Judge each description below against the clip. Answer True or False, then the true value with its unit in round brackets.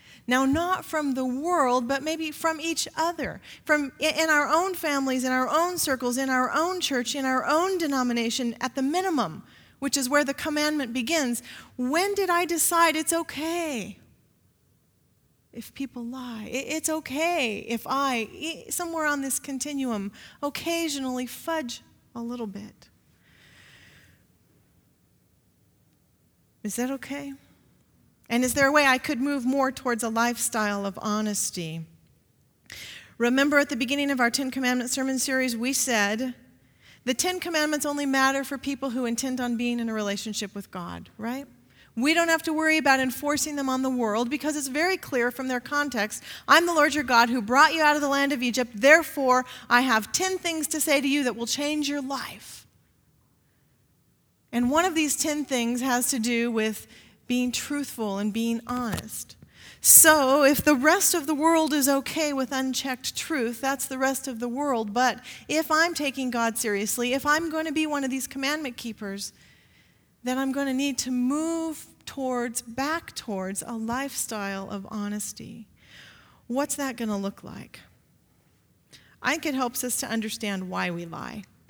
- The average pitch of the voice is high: True (265 Hz)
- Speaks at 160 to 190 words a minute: True (170 wpm)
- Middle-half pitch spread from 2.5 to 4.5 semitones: True (3.8 semitones)